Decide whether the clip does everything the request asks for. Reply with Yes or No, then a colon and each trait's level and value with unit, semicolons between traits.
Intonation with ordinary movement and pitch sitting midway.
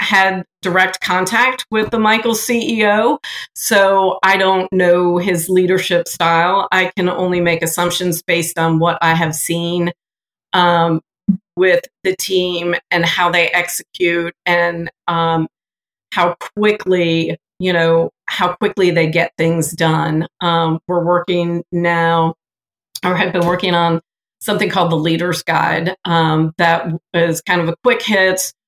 No: narrow, 1.8 semitones; medium, 175 Hz